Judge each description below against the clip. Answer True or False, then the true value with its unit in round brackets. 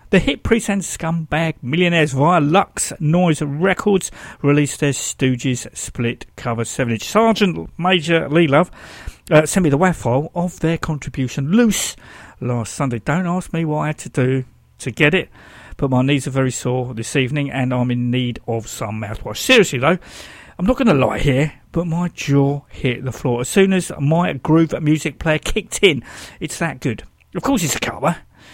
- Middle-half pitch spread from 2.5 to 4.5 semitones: False (5.0 semitones)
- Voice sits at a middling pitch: True (145 Hz)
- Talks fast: False (190 wpm)